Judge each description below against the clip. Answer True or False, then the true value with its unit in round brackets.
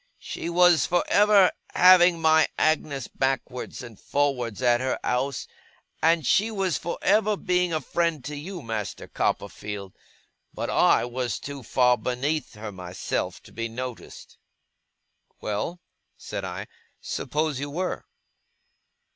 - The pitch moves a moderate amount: False (5.9 semitones)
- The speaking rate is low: True (130 wpm)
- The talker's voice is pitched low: False (145 Hz)